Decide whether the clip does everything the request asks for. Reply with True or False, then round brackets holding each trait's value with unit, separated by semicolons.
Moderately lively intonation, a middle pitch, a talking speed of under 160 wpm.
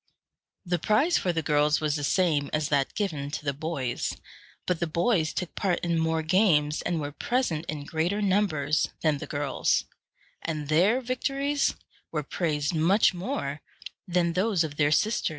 False (4.1 semitones; 160 Hz; 170 wpm)